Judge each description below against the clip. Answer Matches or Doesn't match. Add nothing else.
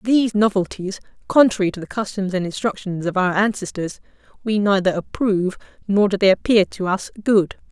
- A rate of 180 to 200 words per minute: Doesn't match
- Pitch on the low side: Doesn't match